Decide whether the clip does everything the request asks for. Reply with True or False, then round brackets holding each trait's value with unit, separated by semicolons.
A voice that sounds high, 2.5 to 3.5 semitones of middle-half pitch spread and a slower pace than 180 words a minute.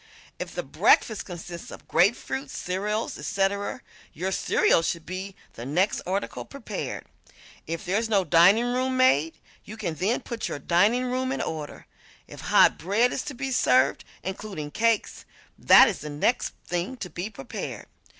False (195 Hz; 5.4 semitones; 155 wpm)